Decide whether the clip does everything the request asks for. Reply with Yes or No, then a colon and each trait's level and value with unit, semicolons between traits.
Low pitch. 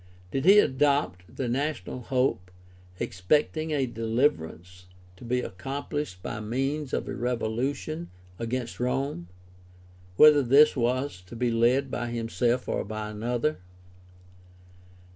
Yes: low, 125 Hz